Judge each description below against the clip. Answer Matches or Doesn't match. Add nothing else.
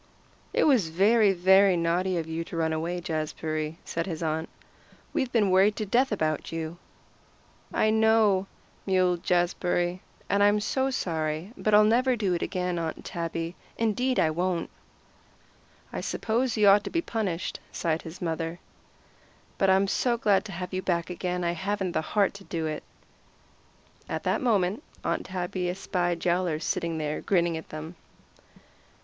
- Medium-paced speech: Matches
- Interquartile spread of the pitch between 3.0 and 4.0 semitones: Matches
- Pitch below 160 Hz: Doesn't match